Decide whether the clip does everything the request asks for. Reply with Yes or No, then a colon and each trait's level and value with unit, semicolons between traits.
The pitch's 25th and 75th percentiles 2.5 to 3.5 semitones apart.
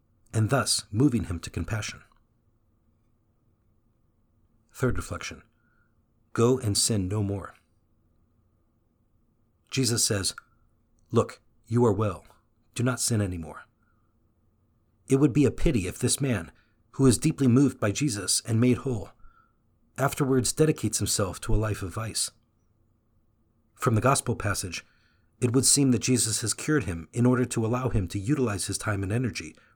Yes: average, 3.0 semitones